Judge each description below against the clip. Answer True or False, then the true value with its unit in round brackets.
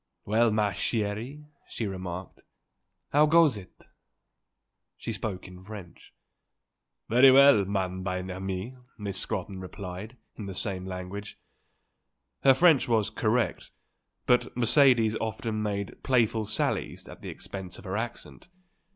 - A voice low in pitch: True (105 Hz)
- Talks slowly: True (125 wpm)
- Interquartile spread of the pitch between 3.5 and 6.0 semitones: True (3.8 semitones)